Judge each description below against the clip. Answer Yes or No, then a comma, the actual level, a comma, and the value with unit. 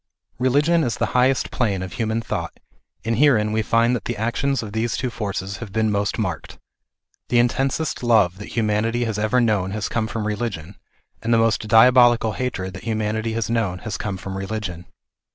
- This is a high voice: No, low, 110 Hz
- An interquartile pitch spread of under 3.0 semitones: Yes, narrow, 2.6 semitones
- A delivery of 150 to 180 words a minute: No, average, 190 wpm